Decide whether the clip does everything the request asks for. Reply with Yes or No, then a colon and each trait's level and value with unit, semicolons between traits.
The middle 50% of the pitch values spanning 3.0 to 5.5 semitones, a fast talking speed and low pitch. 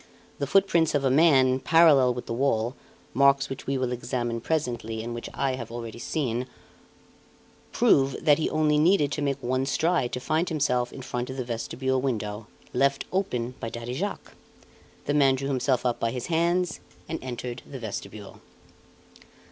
No: average, 3.5 semitones; average, 170 wpm; low, 130 Hz